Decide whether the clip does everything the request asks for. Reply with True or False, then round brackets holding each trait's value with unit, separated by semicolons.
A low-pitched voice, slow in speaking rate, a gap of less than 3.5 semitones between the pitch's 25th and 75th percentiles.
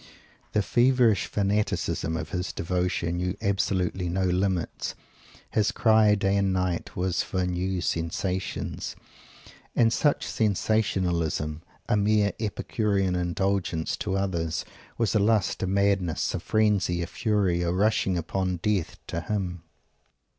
True (95 Hz; 125 wpm; 2.7 semitones)